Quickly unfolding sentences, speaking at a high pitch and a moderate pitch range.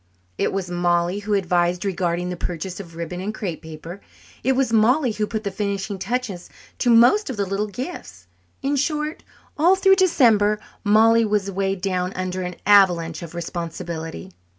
No: average, 170 wpm; high, 195 Hz; average, 4.2 semitones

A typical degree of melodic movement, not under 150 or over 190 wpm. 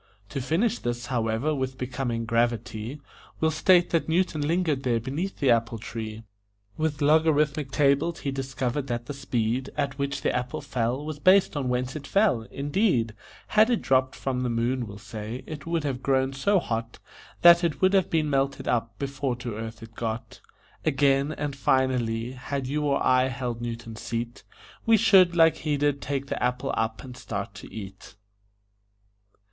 Yes: average, 4.0 semitones; average, 175 wpm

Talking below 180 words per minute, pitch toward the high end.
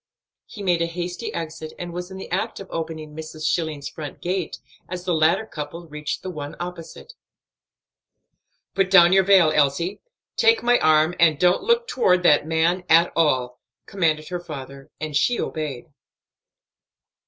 No: average, 160 wpm; medium, 170 Hz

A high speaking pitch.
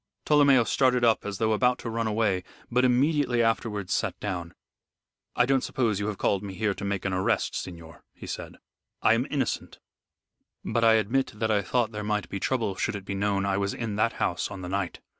No: low, 110 Hz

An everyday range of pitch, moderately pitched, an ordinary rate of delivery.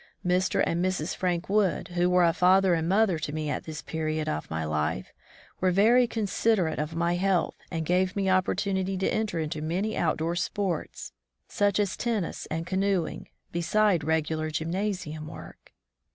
Yes: average, 3.4 semitones; medium, 180 Hz; average, 165 wpm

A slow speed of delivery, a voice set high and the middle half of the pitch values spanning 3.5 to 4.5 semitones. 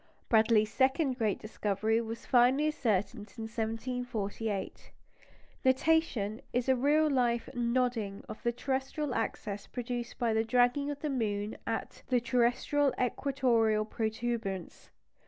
No: slow, 120 wpm; high, 235 Hz; average, 3.0 semitones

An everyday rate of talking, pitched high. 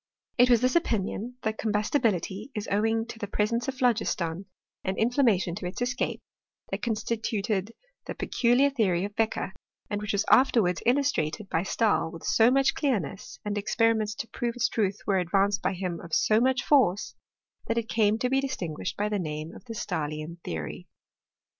Yes: average, 180 wpm; high, 215 Hz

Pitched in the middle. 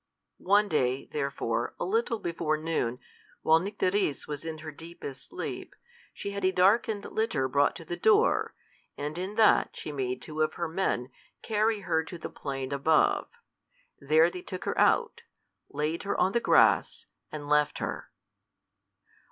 Yes: medium, 165 Hz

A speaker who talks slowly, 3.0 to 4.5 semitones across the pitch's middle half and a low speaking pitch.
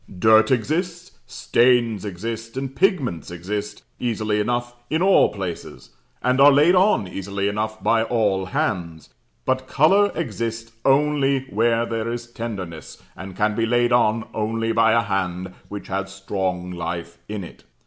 No: average, 150 wpm; average, 4.0 semitones; low, 110 Hz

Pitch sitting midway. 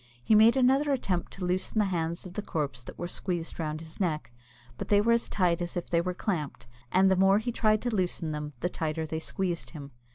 Yes: medium, 180 Hz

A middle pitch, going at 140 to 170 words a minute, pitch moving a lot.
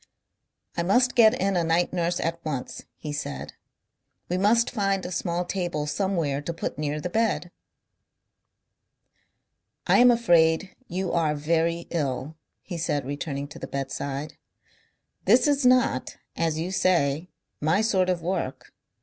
No: medium, 170 Hz; average, 145 wpm; average, 3.9 semitones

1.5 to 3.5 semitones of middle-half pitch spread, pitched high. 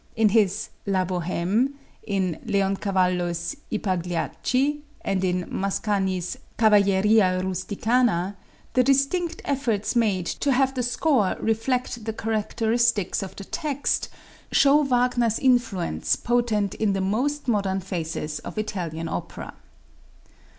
No: average, 4.6 semitones; high, 210 Hz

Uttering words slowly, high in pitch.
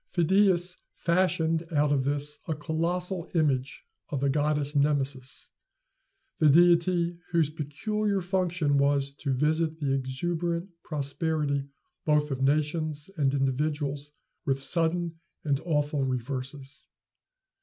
No: slow, 110 wpm; medium, 150 Hz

